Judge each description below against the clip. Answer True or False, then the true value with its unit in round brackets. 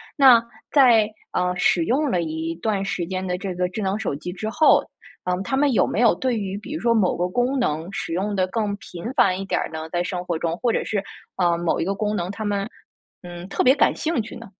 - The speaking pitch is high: True (195 Hz)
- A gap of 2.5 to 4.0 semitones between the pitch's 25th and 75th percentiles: False (4.4 semitones)